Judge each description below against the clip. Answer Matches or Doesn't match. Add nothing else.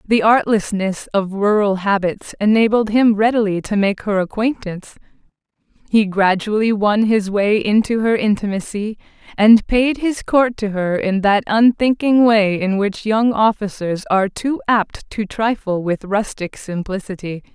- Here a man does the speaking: Doesn't match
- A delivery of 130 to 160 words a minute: Matches